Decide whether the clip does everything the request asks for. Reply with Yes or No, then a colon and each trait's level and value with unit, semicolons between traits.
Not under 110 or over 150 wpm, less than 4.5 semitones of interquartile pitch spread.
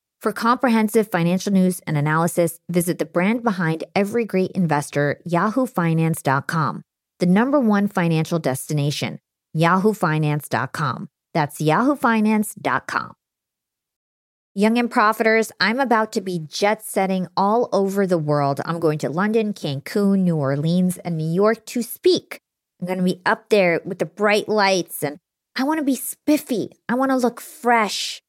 No: average, 140 wpm; average, 5.1 semitones